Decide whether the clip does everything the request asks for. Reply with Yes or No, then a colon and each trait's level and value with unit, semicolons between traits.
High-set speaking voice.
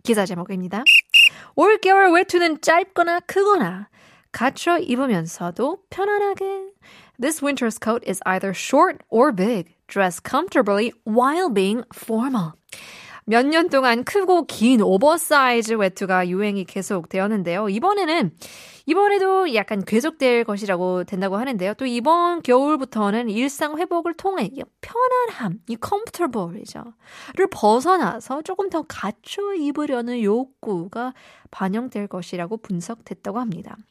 Yes: high, 245 Hz